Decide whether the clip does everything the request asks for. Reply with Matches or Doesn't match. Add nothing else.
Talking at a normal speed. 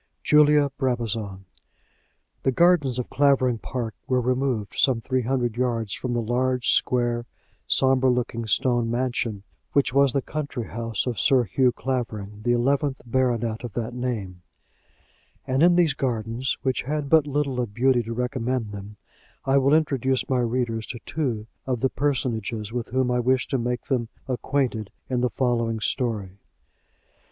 Matches